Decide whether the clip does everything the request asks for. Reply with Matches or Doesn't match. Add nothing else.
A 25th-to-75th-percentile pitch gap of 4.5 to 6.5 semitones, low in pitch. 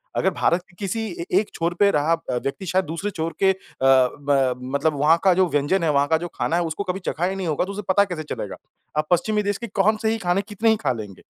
Doesn't match